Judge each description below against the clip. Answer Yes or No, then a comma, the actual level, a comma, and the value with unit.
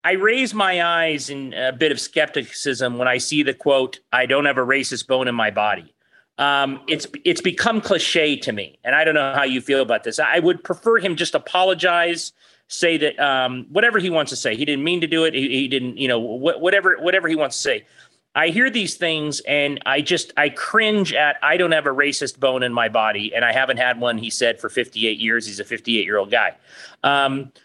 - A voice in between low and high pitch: Yes, medium, 145 Hz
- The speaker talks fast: Yes, fast, 235 wpm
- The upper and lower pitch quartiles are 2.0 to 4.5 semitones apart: No, average, 4.9 semitones